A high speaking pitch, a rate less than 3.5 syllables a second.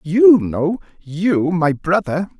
No: medium, 170 Hz; 3.1 syllables/s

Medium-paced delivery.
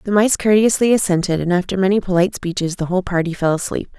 No: fast, 210 wpm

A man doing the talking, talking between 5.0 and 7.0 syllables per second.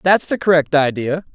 Yes: male; 5.2 syllables/s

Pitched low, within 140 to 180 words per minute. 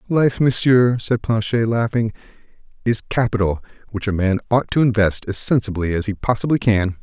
Yes: low, 110 Hz; average, 160 wpm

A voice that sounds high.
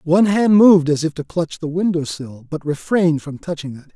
No: medium, 160 Hz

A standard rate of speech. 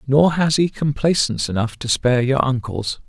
Yes: average, 175 wpm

